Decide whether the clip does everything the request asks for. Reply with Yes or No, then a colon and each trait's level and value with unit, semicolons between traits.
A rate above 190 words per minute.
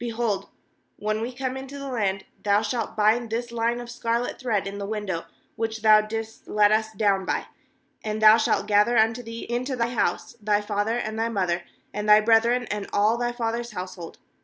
Yes: average, 200 wpm